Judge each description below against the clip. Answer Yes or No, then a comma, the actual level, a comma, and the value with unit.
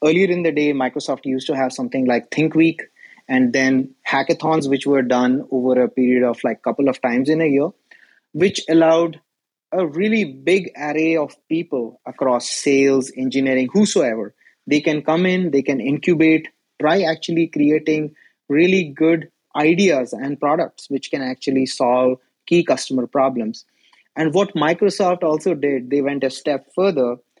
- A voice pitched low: No, medium, 145 Hz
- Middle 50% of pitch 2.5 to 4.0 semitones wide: Yes, average, 3.6 semitones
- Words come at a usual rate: Yes, average, 160 wpm